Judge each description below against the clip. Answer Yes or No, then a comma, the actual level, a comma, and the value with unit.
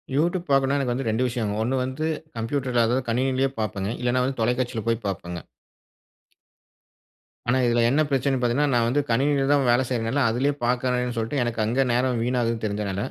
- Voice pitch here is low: Yes, low, 125 Hz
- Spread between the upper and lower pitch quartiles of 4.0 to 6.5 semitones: No, narrow, 2.6 semitones